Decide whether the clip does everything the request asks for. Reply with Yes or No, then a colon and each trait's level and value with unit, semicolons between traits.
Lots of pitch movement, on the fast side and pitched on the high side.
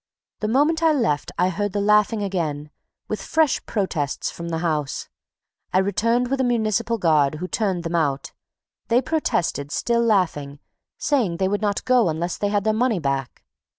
No: wide, 6.0 semitones; average, 175 wpm; high, 200 Hz